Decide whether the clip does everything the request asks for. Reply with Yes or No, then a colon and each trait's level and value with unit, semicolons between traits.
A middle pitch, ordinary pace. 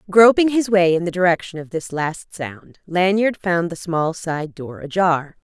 Yes: medium, 175 Hz; average, 185 wpm